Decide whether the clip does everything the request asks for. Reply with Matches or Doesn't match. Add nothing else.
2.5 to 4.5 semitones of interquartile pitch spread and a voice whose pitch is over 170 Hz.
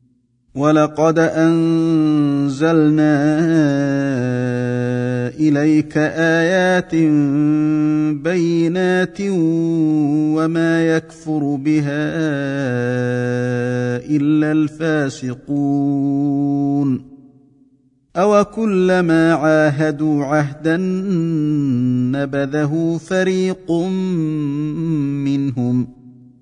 Doesn't match